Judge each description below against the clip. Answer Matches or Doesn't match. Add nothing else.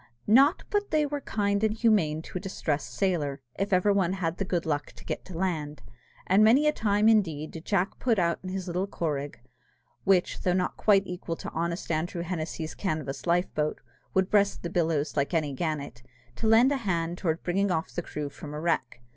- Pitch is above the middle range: Doesn't match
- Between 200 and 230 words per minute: Matches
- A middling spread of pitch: Matches